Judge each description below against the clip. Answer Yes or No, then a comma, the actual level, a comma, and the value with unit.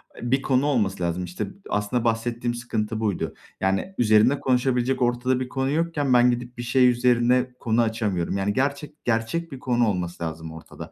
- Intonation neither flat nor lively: Yes, average, 3.3 semitones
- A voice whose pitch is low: Yes, low, 120 Hz